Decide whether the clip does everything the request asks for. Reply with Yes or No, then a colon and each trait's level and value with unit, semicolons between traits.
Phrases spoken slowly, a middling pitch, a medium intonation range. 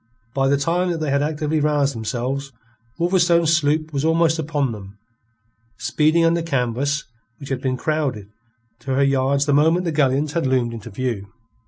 No: average, 170 wpm; medium, 145 Hz; average, 3.4 semitones